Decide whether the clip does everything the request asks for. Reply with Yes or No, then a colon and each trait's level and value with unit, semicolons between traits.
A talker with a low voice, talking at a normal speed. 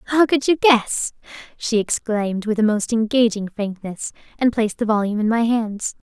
No: high, 225 Hz; average, 180 wpm